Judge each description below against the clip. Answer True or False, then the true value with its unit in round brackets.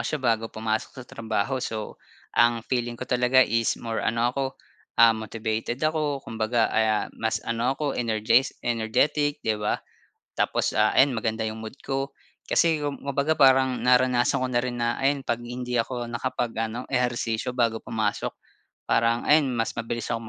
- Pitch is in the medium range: False (120 Hz)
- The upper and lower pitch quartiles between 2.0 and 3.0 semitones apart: True (2.4 semitones)